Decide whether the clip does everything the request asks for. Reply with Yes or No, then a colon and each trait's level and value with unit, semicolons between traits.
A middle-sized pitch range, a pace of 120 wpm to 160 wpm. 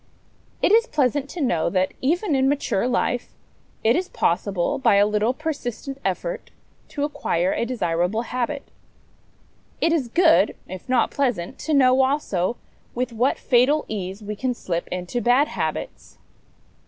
No: wide, 5.7 semitones; average, 150 wpm